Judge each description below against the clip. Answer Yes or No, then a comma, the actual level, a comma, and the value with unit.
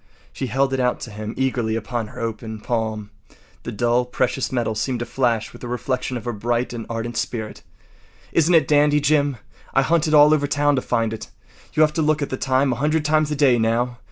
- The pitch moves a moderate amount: Yes, average, 4.0 semitones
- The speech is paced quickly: Yes, fast, 225 wpm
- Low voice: Yes, low, 125 Hz